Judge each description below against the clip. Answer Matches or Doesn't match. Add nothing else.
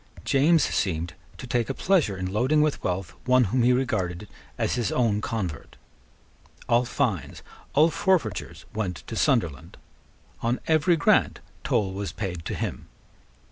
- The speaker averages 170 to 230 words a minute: Doesn't match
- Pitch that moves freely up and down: Matches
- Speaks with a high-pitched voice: Doesn't match